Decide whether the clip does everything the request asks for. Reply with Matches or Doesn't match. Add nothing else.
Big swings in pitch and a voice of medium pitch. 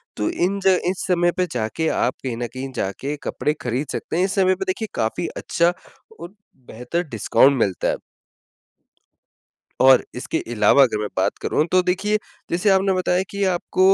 Matches